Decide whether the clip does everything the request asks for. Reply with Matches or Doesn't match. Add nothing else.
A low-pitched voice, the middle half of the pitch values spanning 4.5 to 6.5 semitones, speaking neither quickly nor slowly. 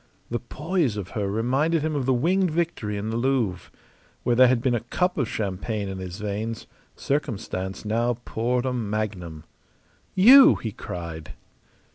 Matches